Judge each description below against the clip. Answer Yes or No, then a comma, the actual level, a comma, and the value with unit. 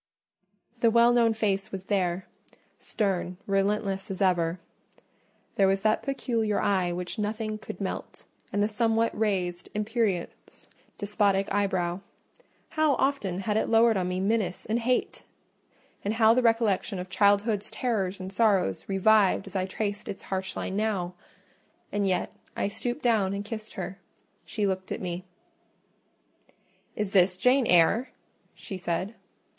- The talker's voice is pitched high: Yes, high, 200 Hz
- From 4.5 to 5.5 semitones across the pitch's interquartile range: No, average, 2.8 semitones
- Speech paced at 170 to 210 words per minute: No, average, 140 wpm